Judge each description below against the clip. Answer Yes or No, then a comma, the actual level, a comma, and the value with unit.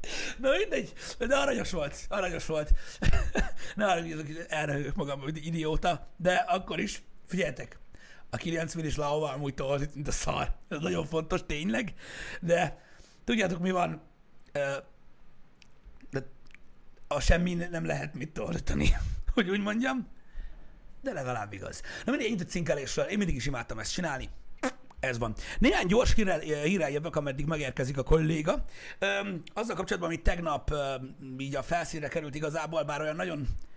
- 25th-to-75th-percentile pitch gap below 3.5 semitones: No, average, 4.2 semitones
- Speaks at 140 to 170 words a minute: Yes, average, 145 wpm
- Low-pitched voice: No, medium, 160 Hz